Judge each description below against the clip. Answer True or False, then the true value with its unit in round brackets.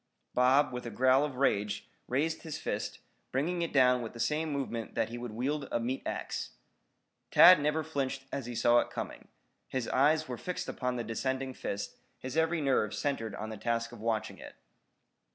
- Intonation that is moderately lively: True (3.8 semitones)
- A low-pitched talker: True (130 Hz)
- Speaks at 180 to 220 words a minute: True (190 wpm)